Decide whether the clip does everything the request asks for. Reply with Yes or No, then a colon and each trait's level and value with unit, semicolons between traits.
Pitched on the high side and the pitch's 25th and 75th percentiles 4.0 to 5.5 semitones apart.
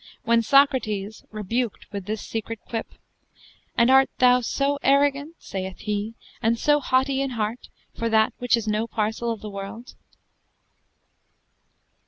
No: high, 230 Hz; average, 3.5 semitones